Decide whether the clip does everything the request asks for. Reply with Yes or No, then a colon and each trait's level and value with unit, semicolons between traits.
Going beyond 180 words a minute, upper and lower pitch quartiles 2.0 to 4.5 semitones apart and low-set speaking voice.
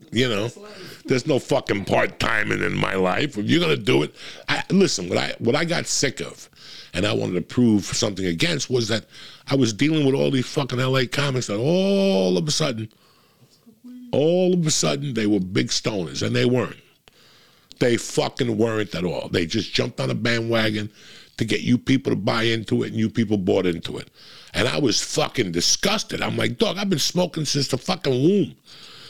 No: average, 200 wpm; wide, 5.6 semitones; low, 125 Hz